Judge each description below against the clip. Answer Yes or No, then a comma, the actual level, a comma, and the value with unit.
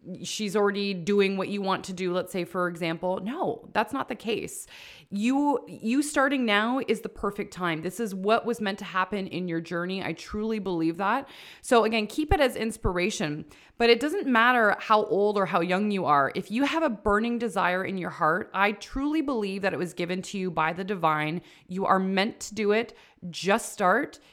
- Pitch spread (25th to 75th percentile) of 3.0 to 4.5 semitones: Yes, average, 3.7 semitones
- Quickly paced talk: Yes, fast, 210 wpm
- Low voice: No, high, 200 Hz